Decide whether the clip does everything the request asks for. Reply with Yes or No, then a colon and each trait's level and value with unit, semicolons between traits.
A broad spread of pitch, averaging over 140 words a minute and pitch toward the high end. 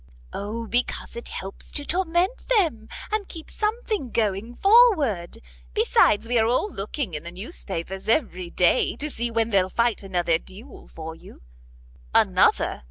Yes: wide, 8.5 semitones; average, 155 wpm; high, 230 Hz